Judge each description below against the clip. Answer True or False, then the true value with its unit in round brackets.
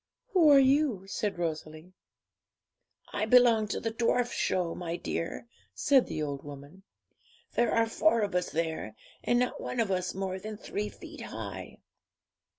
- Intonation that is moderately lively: False (5.8 semitones)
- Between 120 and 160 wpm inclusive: True (155 wpm)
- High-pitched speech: True (205 Hz)